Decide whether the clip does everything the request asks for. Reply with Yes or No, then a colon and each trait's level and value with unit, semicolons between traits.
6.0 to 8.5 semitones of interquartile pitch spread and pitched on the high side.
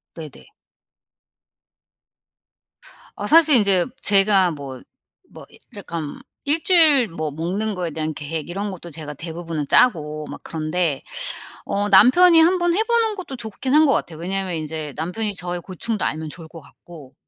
No: wide, 6.5 semitones; medium, 180 Hz